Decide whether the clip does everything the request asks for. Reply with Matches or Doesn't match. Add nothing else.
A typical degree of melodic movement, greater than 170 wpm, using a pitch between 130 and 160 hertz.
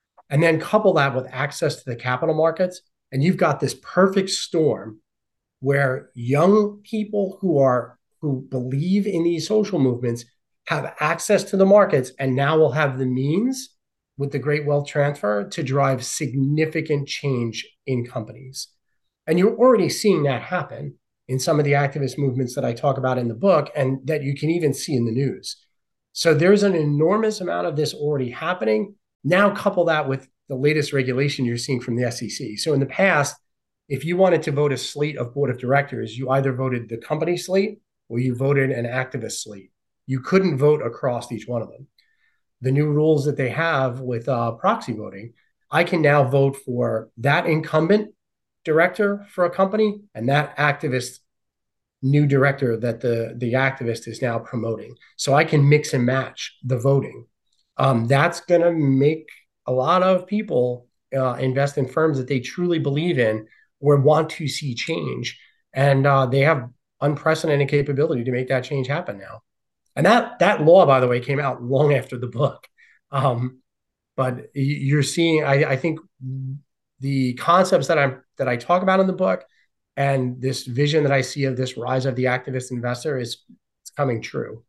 Matches